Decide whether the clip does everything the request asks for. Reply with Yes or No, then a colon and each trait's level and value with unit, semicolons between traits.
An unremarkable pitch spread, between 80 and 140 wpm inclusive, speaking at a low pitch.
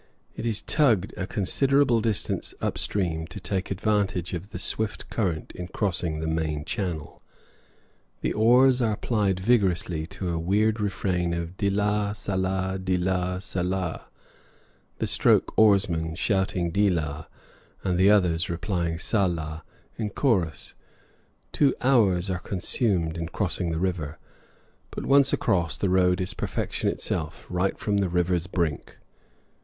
Yes: average, 3.2 semitones; slow, 135 wpm; very low, 95 Hz